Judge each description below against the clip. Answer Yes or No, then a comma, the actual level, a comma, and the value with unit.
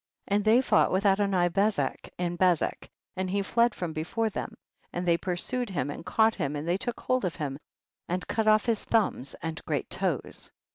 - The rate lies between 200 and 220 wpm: Yes, fast, 205 wpm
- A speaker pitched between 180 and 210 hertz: Yes, high, 190 Hz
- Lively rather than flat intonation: No, average, 4.0 semitones